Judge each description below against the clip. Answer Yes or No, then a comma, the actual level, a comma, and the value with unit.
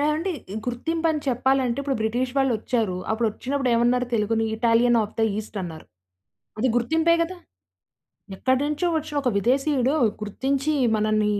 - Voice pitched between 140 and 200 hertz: No, very high, 250 Hz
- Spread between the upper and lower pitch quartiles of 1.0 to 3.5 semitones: No, average, 3.9 semitones